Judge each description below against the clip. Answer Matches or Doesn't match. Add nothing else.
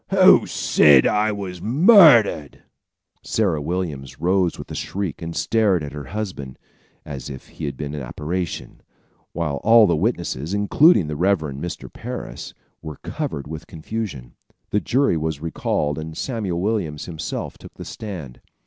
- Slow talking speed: Doesn't match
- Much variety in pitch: Matches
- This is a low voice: Matches